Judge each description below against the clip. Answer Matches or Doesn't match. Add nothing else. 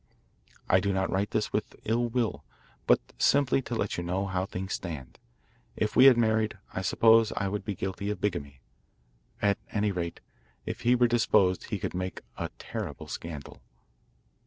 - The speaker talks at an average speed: Matches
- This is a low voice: Matches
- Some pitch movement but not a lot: Matches